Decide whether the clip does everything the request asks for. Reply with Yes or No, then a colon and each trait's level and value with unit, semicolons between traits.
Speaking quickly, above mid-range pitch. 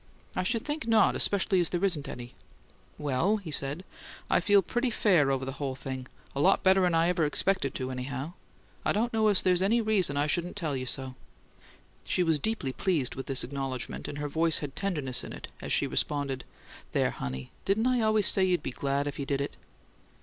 No: fast, 210 wpm; medium, 160 Hz